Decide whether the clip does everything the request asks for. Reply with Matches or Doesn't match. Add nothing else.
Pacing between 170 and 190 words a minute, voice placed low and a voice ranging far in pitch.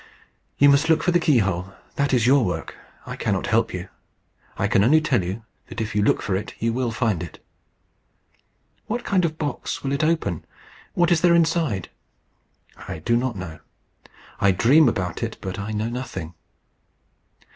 Matches